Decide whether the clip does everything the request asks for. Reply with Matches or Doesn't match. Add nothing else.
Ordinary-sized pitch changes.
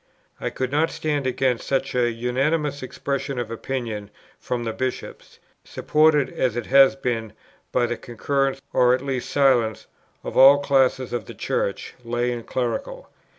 Doesn't match